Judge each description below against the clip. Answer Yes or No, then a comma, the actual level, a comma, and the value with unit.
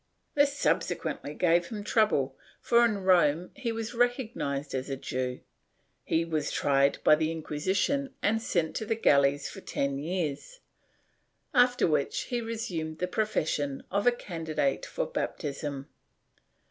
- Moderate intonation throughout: No, wide, 7.7 semitones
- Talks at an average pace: Yes, average, 145 wpm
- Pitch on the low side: No, medium, 170 Hz